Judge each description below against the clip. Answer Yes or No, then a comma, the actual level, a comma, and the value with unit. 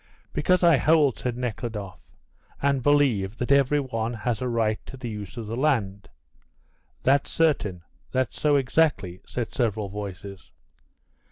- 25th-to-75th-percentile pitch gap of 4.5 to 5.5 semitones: Yes, average, 5.1 semitones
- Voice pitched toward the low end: Yes, low, 120 Hz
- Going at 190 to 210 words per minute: No, average, 145 wpm